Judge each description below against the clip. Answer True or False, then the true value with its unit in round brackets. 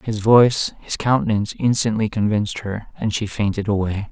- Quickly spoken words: False (145 wpm)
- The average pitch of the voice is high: False (105 Hz)